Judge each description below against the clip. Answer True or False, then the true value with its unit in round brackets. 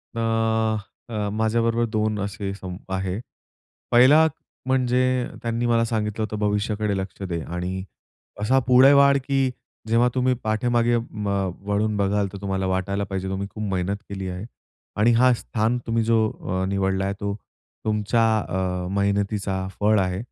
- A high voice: False (105 Hz)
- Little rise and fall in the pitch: False (3.0 semitones)